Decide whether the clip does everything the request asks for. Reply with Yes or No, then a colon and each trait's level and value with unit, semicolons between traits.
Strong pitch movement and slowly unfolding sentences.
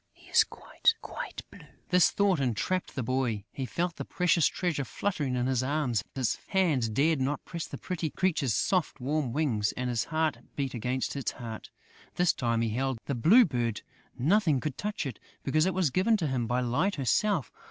No: wide, 5.9 semitones; average, 195 wpm